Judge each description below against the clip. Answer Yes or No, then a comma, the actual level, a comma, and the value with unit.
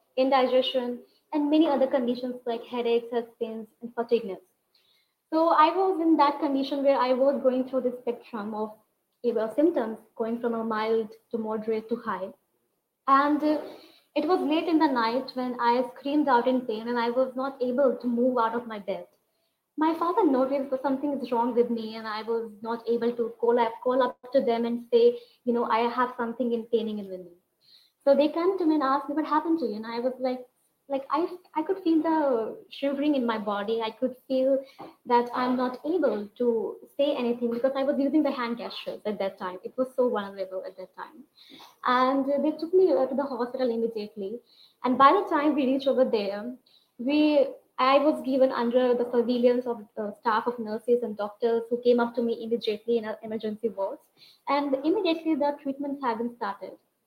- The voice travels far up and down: No, average, 3.3 semitones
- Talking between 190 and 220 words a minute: Yes, average, 200 wpm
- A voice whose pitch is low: No, very high, 250 Hz